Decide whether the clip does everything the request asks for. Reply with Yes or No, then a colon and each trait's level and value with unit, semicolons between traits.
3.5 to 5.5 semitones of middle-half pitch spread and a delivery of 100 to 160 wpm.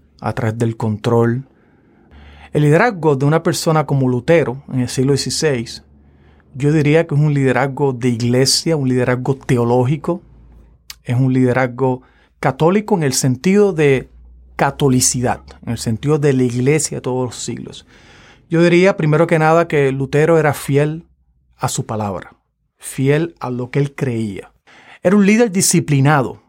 Yes: average, 4.1 semitones; average, 150 wpm